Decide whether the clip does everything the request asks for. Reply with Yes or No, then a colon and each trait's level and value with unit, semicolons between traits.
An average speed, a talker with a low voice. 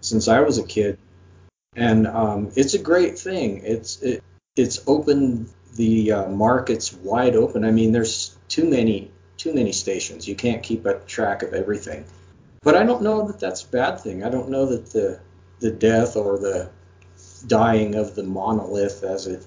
Yes: average, 180 wpm; low, 110 Hz